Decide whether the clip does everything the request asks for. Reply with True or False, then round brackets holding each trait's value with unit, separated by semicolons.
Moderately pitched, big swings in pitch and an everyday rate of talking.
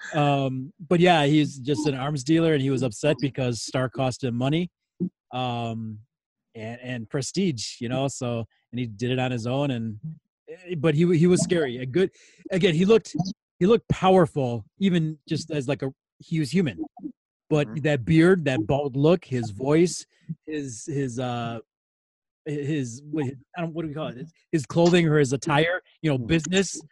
False (150 Hz; 4.5 semitones; 185 wpm)